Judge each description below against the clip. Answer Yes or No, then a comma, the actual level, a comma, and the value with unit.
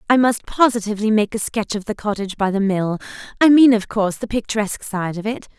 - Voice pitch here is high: Yes, high, 215 Hz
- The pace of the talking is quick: Yes, fast, 215 wpm